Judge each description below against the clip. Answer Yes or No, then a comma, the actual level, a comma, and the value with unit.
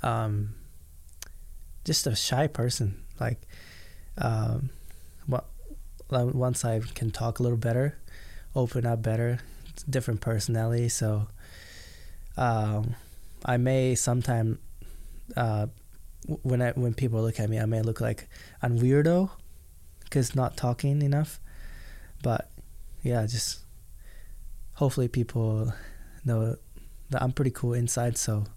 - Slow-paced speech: Yes, slow, 115 wpm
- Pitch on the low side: Yes, low, 110 Hz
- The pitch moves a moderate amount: No, wide, 7.4 semitones